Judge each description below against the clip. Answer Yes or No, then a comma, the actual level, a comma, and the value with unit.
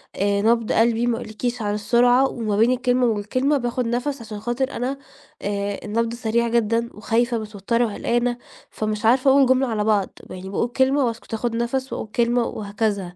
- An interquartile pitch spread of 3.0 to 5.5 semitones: No, narrow, 2.4 semitones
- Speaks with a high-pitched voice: Yes, high, 235 Hz